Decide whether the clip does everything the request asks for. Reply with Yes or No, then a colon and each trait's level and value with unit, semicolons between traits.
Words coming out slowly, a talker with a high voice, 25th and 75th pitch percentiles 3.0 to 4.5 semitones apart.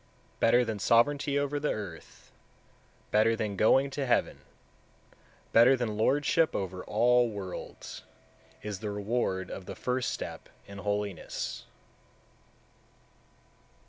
No: slow, 115 wpm; low, 115 Hz; average, 4.0 semitones